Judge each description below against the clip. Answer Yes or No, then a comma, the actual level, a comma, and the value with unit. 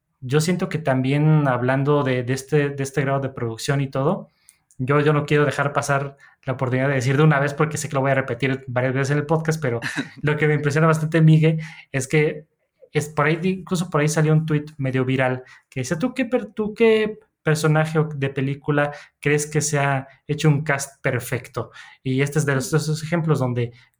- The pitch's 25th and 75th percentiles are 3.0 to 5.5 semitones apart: No, narrow, 2.5 semitones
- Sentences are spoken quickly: Yes, fast, 210 wpm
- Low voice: No, medium, 145 Hz